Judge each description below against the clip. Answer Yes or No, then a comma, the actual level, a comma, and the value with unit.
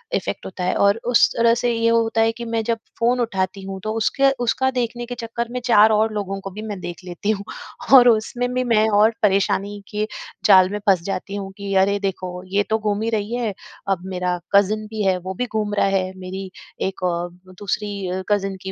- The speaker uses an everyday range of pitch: Yes, average, 3.0 semitones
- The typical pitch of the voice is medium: No, high, 205 Hz